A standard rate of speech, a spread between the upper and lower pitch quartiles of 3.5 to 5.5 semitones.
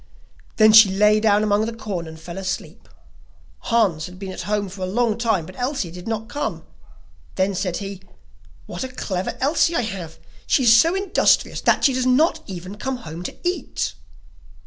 Yes: average, 190 wpm; average, 4.5 semitones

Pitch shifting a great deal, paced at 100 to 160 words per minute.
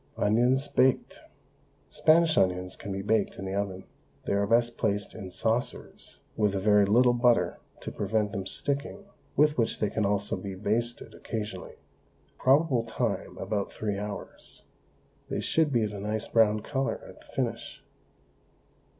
No: average, 3.3 semitones; average, 155 wpm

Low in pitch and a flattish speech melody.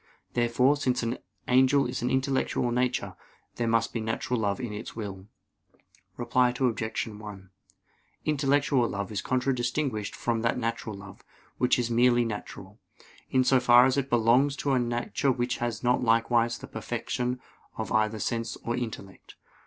Yes: low, 120 Hz; narrow, 2.1 semitones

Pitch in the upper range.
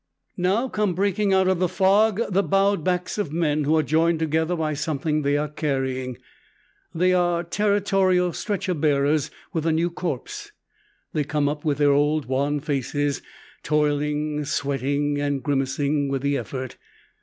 No: medium, 155 Hz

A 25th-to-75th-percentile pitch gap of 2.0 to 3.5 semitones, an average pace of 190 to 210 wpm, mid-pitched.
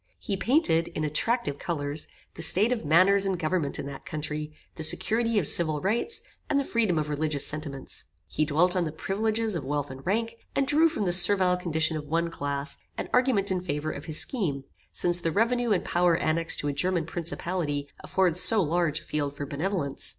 No: average, 4.7 semitones; average, 200 wpm; medium, 170 Hz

